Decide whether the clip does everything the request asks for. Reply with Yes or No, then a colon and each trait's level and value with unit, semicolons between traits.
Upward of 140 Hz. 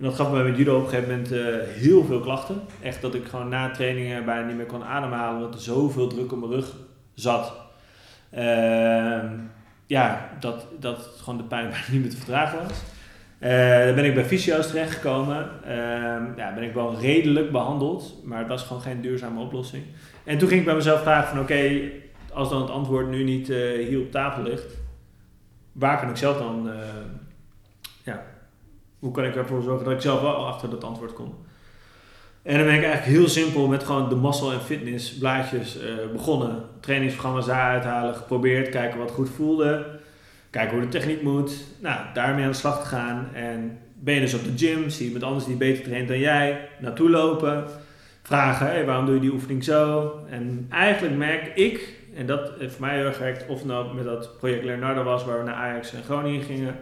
No: low, 130 Hz